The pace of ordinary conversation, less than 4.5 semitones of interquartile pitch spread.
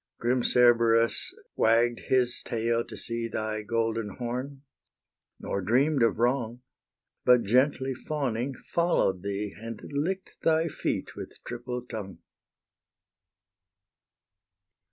No: slow, 105 wpm; narrow, 2.5 semitones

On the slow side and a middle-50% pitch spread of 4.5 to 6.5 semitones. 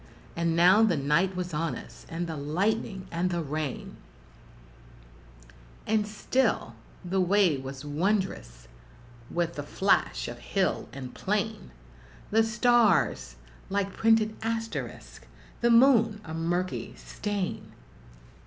Yes: slow, 115 wpm; wide, 5.5 semitones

